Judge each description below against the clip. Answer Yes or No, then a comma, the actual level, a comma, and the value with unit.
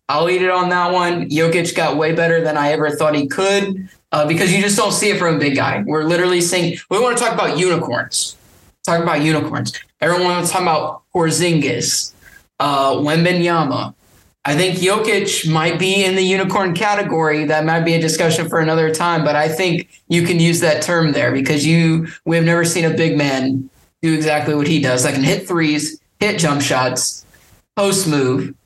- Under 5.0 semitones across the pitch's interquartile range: Yes, average, 2.8 semitones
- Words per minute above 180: Yes, average, 200 wpm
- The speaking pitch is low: No, medium, 165 Hz